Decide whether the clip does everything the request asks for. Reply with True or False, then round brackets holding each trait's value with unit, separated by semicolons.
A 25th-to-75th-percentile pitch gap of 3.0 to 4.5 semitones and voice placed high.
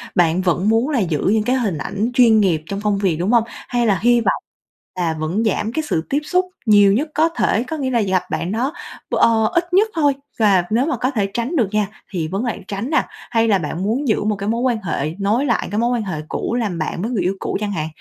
True (4.2 semitones; 215 Hz)